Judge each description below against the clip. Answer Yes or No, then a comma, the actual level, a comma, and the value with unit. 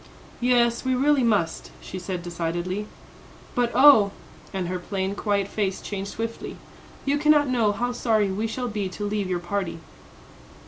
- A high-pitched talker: Yes, high, 205 Hz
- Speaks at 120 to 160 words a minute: Yes, average, 155 wpm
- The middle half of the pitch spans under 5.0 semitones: Yes, average, 4.3 semitones